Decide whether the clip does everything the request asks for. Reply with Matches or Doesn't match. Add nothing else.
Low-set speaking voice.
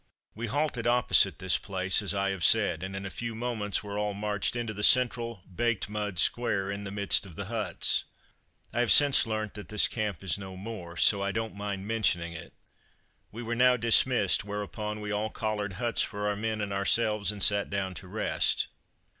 Matches